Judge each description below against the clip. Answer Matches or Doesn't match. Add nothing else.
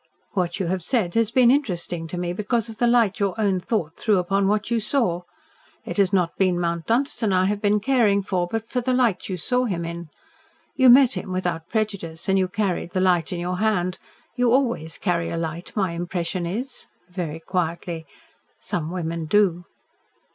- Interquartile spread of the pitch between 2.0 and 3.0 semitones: Doesn't match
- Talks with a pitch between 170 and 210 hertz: Matches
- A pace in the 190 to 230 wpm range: Matches